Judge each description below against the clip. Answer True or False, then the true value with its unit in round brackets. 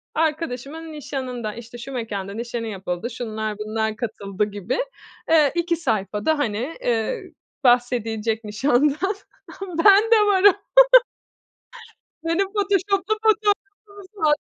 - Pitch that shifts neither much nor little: False (7.4 semitones)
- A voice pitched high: True (250 Hz)